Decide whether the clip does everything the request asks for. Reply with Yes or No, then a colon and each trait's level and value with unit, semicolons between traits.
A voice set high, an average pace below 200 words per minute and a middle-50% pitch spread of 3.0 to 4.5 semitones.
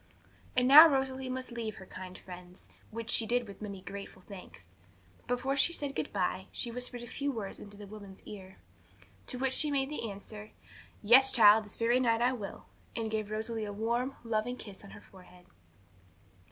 Yes: high, 225 Hz; average, 185 wpm; average, 3.9 semitones